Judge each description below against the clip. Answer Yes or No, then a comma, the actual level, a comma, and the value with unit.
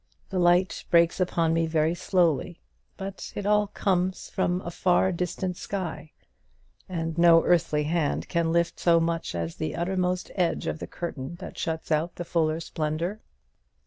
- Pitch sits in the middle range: Yes, medium, 170 Hz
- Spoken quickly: No, average, 160 wpm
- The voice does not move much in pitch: Yes, narrow, 1.9 semitones